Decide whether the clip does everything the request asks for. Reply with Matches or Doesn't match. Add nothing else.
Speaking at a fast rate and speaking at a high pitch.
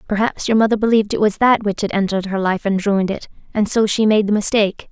Matches